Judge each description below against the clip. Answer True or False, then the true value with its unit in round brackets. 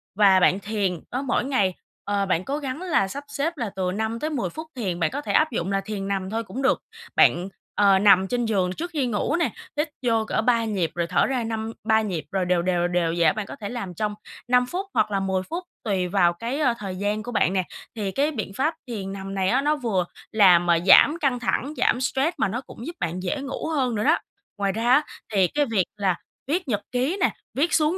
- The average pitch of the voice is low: False (220 Hz)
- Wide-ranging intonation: True (5.8 semitones)